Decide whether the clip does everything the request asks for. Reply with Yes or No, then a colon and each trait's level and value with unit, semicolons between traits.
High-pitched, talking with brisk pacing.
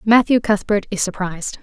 No: high, 205 Hz; average, 150 wpm